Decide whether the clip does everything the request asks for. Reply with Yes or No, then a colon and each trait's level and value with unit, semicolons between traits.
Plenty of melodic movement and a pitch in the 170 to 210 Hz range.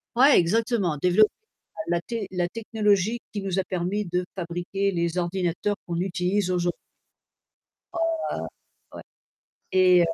No: average, 2.8 semitones; medium, 185 Hz